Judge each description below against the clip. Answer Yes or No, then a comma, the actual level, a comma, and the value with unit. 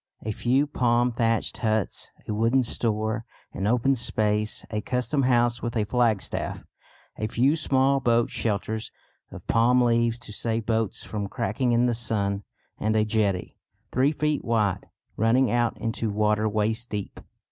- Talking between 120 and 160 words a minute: Yes, average, 155 wpm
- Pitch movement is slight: Yes, narrow, 2.2 semitones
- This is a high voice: No, low, 115 Hz